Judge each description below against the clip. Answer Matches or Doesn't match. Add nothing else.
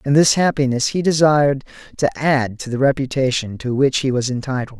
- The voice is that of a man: Matches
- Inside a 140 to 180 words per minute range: Doesn't match